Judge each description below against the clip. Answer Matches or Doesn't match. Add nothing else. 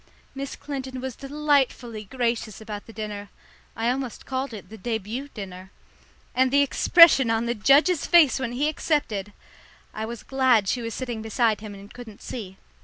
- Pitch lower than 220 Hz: Doesn't match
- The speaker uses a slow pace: Doesn't match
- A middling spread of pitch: Matches